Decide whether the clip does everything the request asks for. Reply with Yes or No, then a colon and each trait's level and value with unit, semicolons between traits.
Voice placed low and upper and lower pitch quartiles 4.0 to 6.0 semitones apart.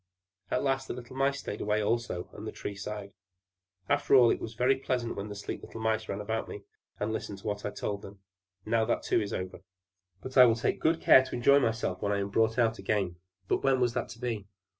No: low, 110 Hz; average, 3.5 semitones